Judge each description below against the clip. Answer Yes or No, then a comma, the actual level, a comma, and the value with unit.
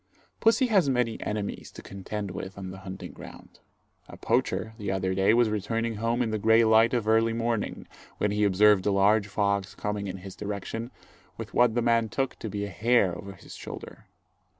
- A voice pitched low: Yes, low, 105 Hz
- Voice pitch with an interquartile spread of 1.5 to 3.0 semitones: Yes, average, 2.7 semitones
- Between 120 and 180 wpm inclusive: No, average, 195 wpm